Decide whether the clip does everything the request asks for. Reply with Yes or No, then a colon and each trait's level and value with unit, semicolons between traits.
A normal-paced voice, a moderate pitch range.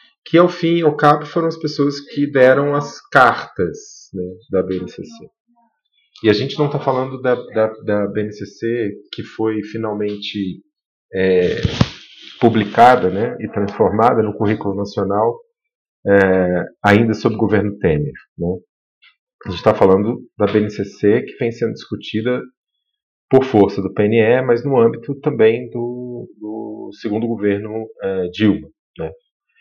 No: average, 140 wpm; wide, 6.3 semitones